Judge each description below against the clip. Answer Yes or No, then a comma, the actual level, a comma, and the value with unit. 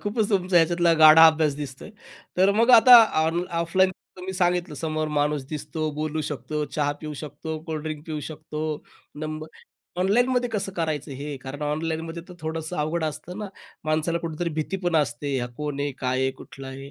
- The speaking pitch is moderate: Yes, medium, 155 Hz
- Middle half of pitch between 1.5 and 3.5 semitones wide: Yes, average, 2.8 semitones